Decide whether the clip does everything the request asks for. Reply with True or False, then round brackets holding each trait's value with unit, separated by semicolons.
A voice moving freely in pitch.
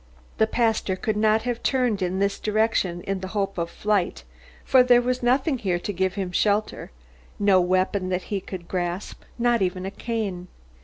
False (3.3 semitones)